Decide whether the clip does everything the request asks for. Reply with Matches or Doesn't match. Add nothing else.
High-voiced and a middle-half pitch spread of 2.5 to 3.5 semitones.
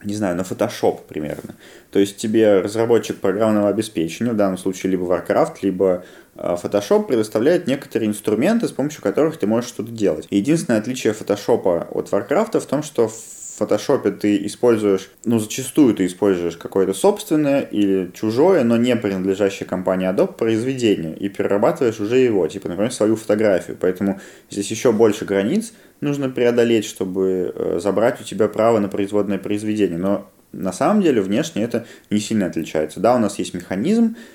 Doesn't match